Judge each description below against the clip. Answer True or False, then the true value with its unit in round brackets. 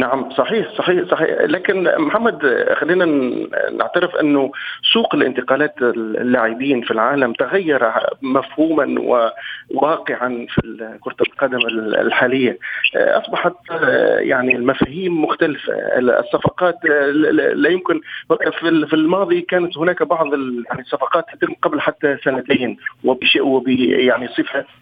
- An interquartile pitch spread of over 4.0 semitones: True (5.5 semitones)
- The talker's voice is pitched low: False (145 Hz)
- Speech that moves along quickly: False (100 wpm)